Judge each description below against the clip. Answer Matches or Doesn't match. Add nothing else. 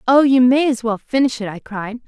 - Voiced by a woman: Matches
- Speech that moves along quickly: Matches